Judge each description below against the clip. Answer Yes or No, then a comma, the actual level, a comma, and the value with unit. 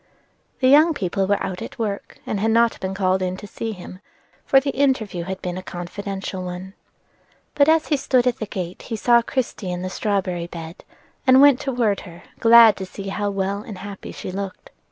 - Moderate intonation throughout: Yes, average, 4.1 semitones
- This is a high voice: Yes, high, 200 Hz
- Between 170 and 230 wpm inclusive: Yes, fast, 205 wpm